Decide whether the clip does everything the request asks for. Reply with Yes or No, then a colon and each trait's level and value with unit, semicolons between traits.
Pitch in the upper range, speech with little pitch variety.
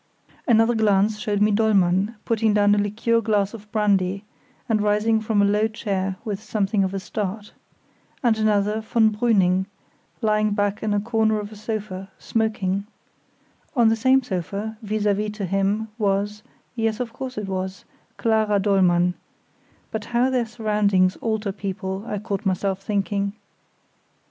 Yes: high, 210 Hz; narrow, 1.9 semitones